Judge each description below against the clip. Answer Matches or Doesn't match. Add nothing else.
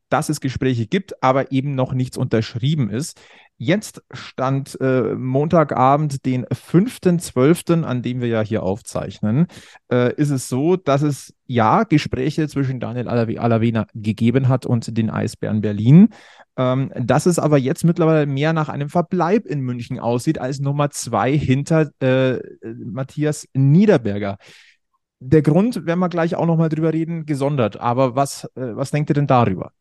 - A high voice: Doesn't match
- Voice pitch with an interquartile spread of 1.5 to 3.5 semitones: Doesn't match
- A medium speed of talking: Matches